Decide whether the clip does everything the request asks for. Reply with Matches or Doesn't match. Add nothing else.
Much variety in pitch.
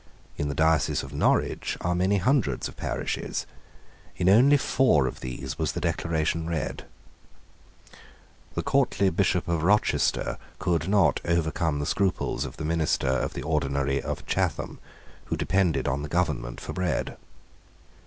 Doesn't match